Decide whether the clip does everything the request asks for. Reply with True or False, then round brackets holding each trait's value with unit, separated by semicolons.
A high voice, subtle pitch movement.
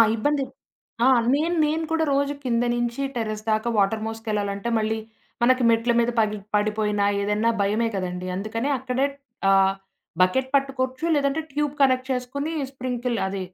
False (235 Hz; 4.3 semitones)